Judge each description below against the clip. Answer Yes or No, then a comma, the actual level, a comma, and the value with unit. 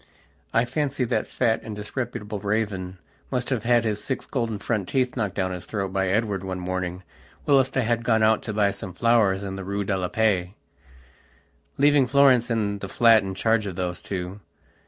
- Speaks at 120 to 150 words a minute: No, average, 195 wpm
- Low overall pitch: Yes, low, 105 Hz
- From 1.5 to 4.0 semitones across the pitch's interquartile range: Yes, average, 3.6 semitones